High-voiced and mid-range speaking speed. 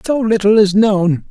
Yes: high, 205 Hz; average, 185 wpm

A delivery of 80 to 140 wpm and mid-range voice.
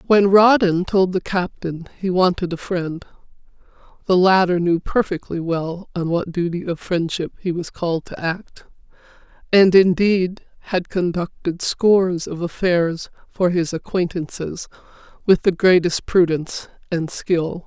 Yes: slow, 135 wpm; medium, 175 Hz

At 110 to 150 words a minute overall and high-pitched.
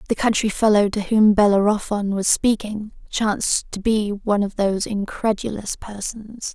Yes: average, 145 wpm; high, 210 Hz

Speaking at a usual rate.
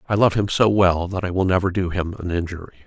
No: fast, 270 wpm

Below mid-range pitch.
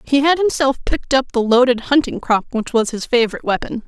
No: very high, 250 Hz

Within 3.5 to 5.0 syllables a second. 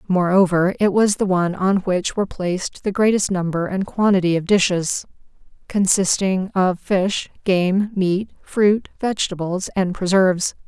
Yes: 4.5 syllables/s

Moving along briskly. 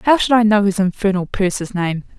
Yes: fast, 220 wpm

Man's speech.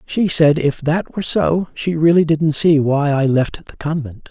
Yes: male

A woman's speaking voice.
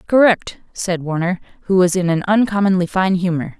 Yes: female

